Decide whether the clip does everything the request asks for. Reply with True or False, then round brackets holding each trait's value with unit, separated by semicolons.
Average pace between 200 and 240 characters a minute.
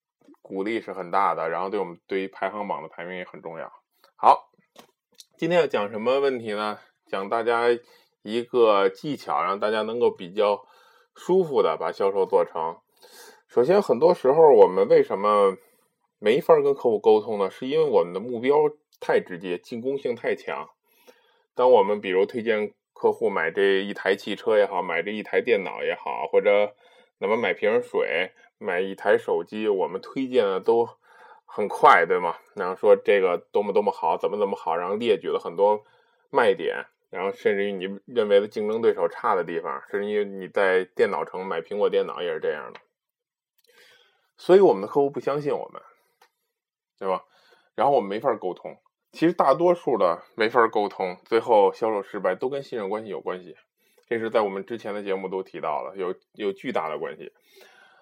False (275 characters per minute)